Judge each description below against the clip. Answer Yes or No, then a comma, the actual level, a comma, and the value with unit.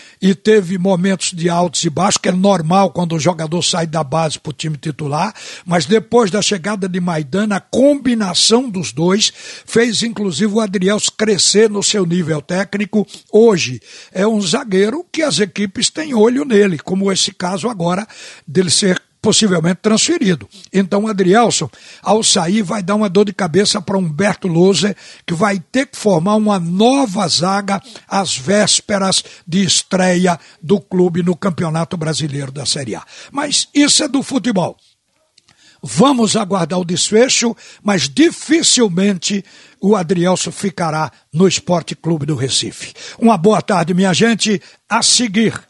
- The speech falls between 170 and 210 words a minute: No, average, 155 wpm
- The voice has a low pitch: No, high, 195 Hz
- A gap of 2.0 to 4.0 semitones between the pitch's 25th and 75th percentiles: Yes, average, 3.4 semitones